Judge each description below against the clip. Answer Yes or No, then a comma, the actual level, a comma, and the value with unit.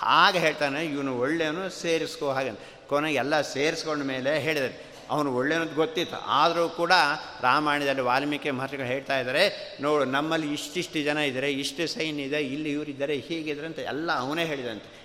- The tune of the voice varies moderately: No, narrow, 2.3 semitones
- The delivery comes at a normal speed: No, fast, 150 wpm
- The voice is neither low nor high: Yes, medium, 150 Hz